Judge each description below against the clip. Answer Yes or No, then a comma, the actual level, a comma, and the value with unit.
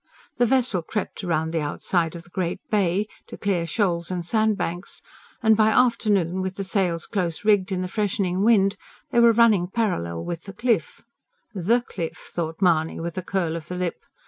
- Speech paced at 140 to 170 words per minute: No, average, 185 wpm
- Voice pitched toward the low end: No, medium, 185 Hz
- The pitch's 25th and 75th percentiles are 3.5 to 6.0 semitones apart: Yes, average, 3.9 semitones